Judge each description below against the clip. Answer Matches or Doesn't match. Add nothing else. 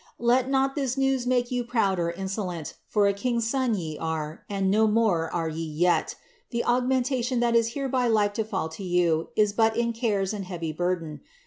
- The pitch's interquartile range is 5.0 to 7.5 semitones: Matches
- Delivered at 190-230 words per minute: Matches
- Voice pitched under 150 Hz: Doesn't match